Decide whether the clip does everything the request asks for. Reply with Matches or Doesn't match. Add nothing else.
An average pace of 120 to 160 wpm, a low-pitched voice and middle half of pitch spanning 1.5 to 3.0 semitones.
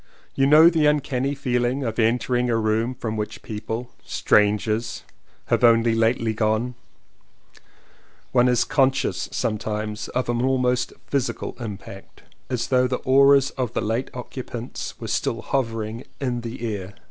Matches